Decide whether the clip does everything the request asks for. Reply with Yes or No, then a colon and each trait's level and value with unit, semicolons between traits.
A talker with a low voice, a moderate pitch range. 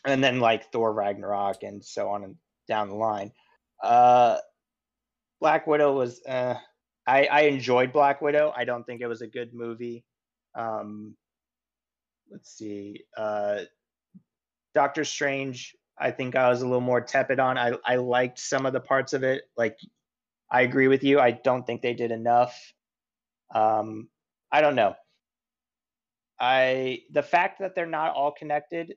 Yes: low, 125 Hz; average, 3.4 semitones